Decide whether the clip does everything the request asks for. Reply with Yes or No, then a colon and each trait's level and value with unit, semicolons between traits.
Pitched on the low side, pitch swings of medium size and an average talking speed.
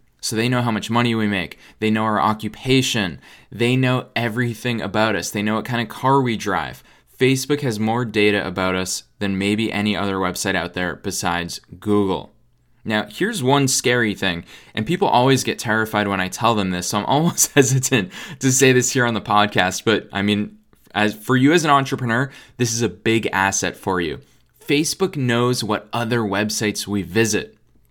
Yes: low, 110 Hz; average, 3.6 semitones; average, 190 wpm